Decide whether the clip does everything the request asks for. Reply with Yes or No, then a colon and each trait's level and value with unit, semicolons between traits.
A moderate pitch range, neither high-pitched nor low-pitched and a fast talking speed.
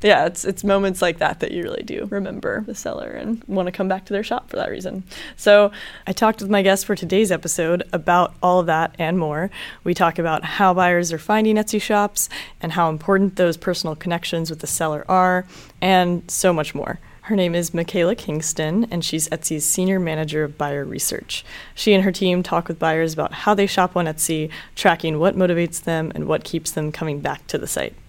Yes: average, 3.3 semitones; medium, 180 Hz; fast, 215 wpm